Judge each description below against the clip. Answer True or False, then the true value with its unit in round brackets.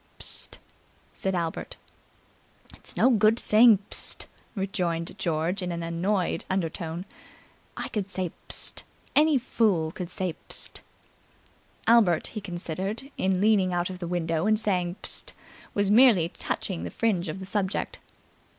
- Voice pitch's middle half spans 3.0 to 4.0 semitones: True (3.4 semitones)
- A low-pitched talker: False (185 Hz)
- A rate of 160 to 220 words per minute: False (140 wpm)